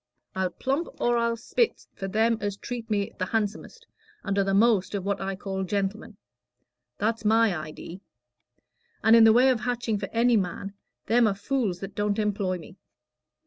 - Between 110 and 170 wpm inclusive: No, average, 180 wpm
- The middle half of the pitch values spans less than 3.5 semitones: Yes, average, 2.9 semitones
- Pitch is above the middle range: Yes, high, 210 Hz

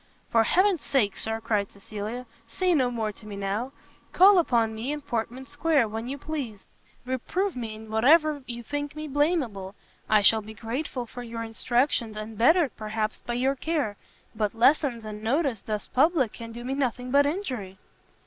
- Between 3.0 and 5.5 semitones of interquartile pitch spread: Yes, average, 4.7 semitones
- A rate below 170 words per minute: No, average, 175 wpm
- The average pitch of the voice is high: Yes, high, 240 Hz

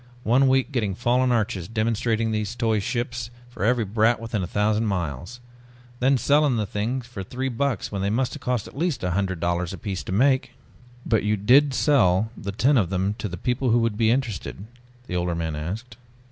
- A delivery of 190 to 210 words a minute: Yes, average, 200 wpm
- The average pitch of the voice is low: Yes, low, 110 Hz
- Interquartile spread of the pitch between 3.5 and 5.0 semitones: Yes, average, 4.0 semitones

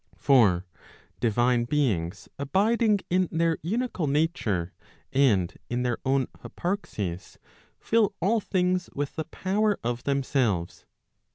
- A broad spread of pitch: Yes, wide, 7.7 semitones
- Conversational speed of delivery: No, slow, 110 wpm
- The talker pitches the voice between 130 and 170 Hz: Yes, medium, 140 Hz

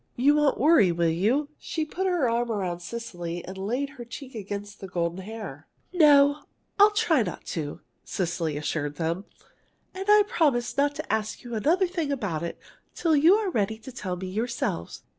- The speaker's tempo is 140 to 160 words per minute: No, average, 180 wpm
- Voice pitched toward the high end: Yes, high, 230 Hz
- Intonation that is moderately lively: No, wide, 8.5 semitones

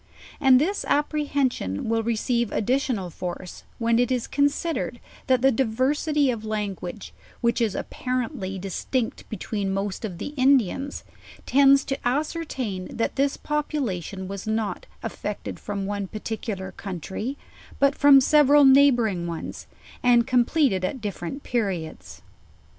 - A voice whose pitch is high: Yes, high, 235 Hz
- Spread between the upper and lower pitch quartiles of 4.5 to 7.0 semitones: Yes, wide, 5.6 semitones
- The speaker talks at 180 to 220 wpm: No, slow, 135 wpm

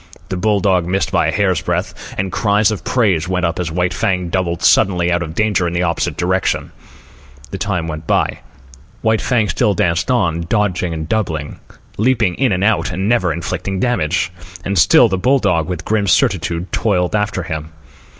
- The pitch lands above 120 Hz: No, very low, 95 Hz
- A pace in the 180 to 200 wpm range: Yes, average, 190 wpm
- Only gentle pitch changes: No, average, 3.3 semitones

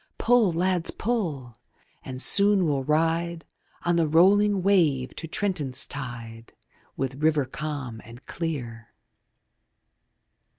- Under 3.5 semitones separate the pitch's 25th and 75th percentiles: No, wide, 5.5 semitones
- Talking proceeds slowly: Yes, slow, 110 wpm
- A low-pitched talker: No, medium, 155 Hz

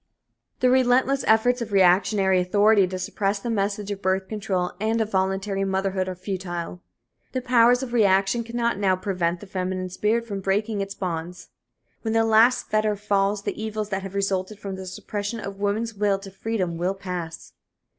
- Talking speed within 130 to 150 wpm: No, average, 175 wpm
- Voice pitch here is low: No, high, 200 Hz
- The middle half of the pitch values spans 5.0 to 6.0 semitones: No, narrow, 2.6 semitones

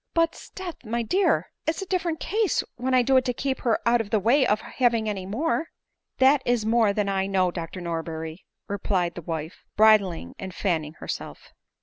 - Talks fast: Yes, fast, 210 wpm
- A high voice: Yes, high, 220 Hz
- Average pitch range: No, wide, 6.0 semitones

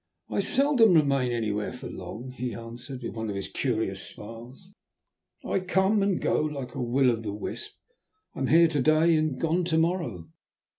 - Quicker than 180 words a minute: Yes, average, 190 wpm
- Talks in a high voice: No, low, 135 Hz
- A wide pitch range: Yes, wide, 6.6 semitones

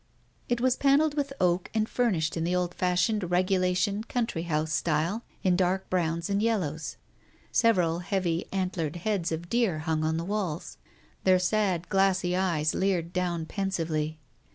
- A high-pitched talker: No, medium, 180 Hz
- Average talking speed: Yes, average, 155 wpm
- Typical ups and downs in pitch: Yes, average, 3.3 semitones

